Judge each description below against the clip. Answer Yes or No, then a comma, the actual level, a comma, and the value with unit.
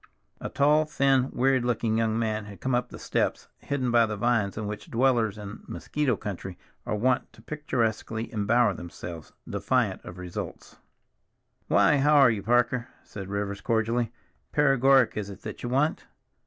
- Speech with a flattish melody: No, average, 3.8 semitones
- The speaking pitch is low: Yes, low, 115 Hz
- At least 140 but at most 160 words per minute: No, average, 170 wpm